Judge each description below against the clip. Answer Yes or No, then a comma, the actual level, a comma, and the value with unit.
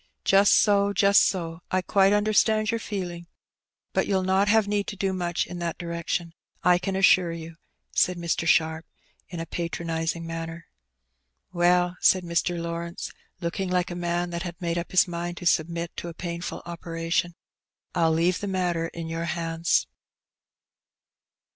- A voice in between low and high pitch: Yes, medium, 175 Hz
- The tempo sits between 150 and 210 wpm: Yes, average, 165 wpm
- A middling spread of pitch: No, narrow, 1.8 semitones